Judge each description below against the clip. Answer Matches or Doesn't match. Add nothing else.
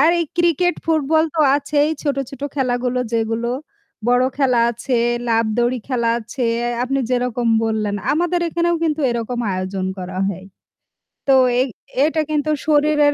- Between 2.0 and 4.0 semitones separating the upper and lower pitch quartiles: Doesn't match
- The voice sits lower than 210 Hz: Doesn't match